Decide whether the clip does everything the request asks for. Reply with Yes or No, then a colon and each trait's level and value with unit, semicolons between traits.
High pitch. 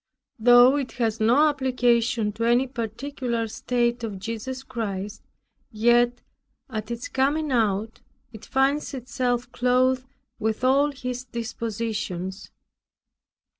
Yes: high, 240 Hz